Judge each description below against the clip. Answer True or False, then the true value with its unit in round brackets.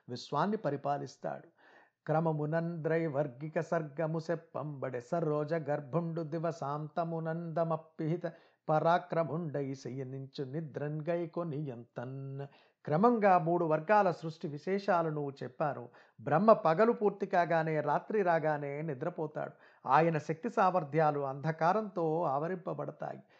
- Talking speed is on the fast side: False (75 wpm)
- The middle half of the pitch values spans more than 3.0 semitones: False (2.6 semitones)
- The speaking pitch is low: False (160 Hz)